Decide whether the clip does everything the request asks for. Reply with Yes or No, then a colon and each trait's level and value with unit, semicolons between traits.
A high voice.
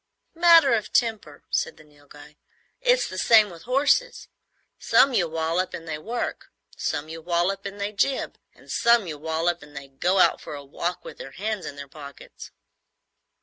No: medium, 175 Hz